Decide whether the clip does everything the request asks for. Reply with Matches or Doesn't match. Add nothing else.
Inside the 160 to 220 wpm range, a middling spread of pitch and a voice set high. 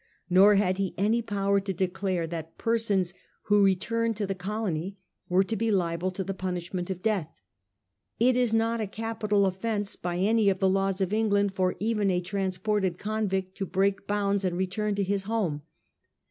Doesn't match